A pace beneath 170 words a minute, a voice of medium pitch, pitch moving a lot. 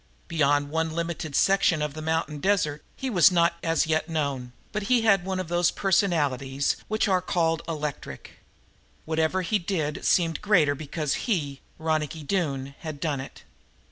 No: average, 160 wpm; medium, 160 Hz; average, 3.5 semitones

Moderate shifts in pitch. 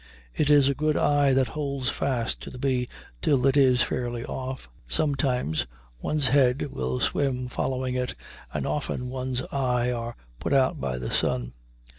No: narrow, 2.1 semitones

